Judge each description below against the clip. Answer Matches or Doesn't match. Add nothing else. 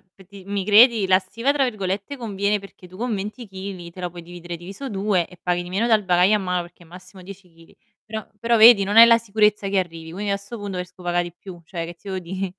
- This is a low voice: Doesn't match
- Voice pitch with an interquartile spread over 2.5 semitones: Matches